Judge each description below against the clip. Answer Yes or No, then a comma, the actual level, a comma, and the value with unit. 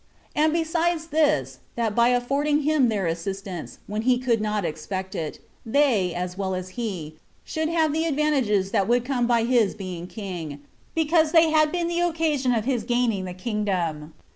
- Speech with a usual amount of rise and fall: No, wide, 8.2 semitones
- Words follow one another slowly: No, average, 175 wpm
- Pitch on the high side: Yes, high, 235 Hz